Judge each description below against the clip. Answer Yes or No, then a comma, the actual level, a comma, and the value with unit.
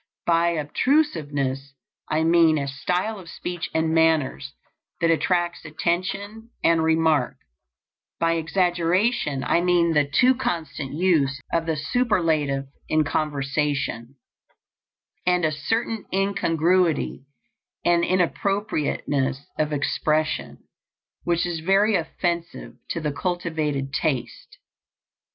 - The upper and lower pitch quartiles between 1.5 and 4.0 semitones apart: Yes, average, 3.2 semitones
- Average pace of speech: No, slow, 105 wpm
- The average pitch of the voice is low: No, medium, 165 Hz